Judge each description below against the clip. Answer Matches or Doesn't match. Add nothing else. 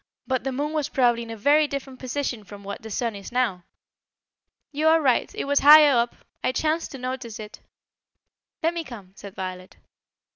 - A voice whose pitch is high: Matches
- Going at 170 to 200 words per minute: Matches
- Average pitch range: Matches